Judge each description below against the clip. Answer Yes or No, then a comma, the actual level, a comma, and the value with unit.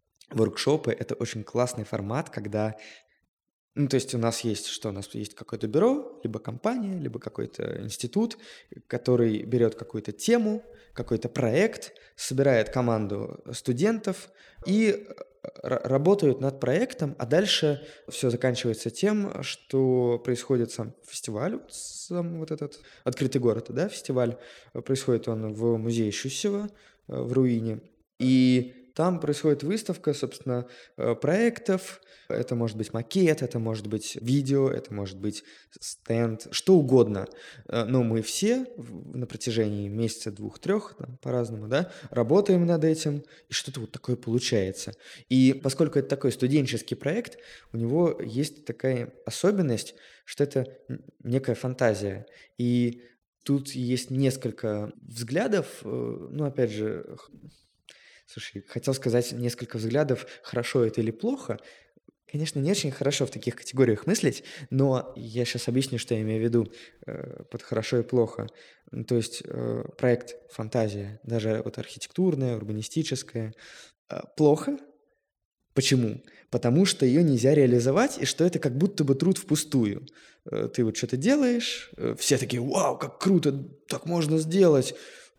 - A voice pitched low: Yes, low, 125 Hz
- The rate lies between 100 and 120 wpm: No, average, 130 wpm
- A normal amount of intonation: Yes, average, 4.9 semitones